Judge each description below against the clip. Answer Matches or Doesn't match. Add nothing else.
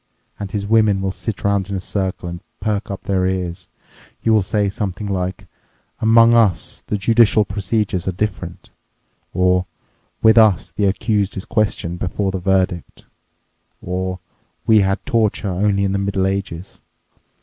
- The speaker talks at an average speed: Matches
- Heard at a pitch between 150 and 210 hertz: Doesn't match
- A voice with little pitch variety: Matches